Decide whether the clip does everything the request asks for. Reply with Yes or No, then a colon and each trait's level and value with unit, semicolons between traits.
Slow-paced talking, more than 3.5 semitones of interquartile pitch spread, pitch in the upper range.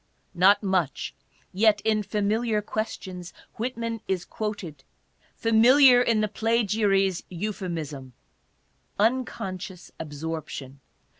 Yes: slow, 95 wpm; average, 3.9 semitones; high, 205 Hz